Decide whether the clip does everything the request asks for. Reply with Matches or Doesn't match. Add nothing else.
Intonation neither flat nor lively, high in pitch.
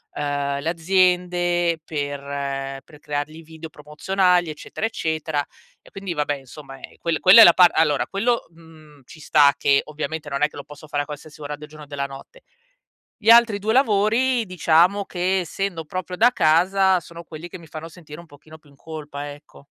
Doesn't match